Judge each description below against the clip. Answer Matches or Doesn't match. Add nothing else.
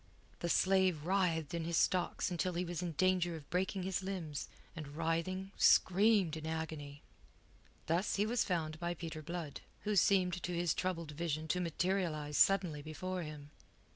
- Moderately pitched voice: Matches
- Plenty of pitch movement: Doesn't match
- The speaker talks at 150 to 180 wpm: Matches